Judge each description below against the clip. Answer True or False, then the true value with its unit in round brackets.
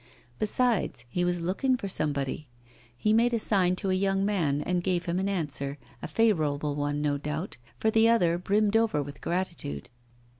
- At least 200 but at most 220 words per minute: False (180 wpm)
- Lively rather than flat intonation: True (5.8 semitones)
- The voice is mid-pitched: True (180 Hz)